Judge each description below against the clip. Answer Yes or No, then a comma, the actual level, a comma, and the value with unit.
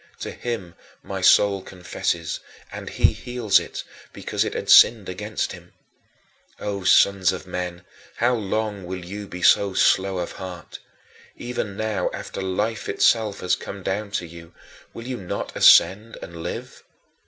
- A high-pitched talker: No, low, 100 Hz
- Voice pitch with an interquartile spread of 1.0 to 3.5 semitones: Yes, average, 2.9 semitones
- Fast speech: No, average, 155 wpm